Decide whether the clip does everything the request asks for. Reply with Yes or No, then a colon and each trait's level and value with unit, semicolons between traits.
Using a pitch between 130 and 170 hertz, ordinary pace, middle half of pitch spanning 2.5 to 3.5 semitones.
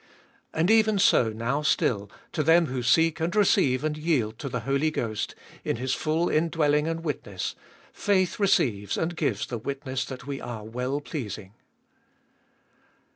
No: medium, 140 Hz; average, 155 wpm; average, 5.2 semitones